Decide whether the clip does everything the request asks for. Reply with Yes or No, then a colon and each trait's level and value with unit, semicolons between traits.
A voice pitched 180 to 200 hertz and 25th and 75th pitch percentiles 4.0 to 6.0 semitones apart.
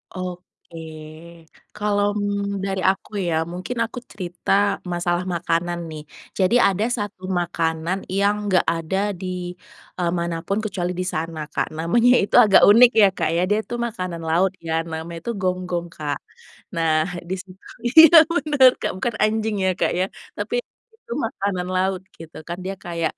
No: medium, 185 Hz; average, 3.3 semitones